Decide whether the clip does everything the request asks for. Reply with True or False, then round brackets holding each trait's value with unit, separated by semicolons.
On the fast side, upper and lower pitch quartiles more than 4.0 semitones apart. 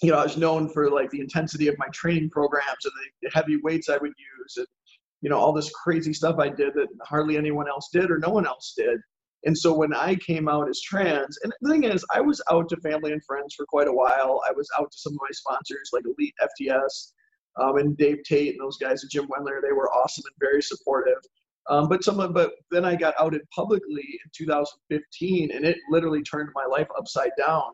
True (235 wpm; 4.4 semitones)